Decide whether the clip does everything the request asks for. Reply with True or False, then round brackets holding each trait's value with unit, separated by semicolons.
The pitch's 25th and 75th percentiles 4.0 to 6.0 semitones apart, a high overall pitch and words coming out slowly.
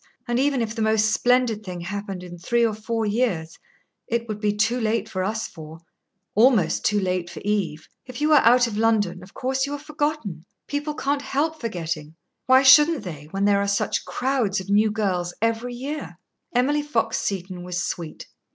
False (5.2 semitones; 220 Hz; 190 wpm)